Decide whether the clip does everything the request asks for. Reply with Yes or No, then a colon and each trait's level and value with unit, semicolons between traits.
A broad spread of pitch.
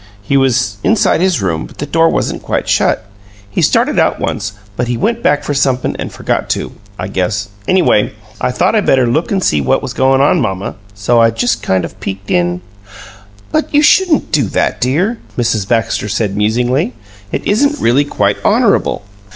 Yes: wide, 6.4 semitones